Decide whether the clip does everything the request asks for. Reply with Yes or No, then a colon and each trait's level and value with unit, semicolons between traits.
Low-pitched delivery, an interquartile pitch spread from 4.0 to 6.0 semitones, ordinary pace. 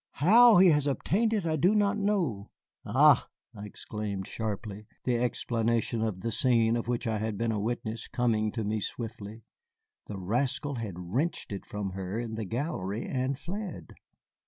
Yes: low, 115 Hz; average, 5.2 semitones; average, 165 wpm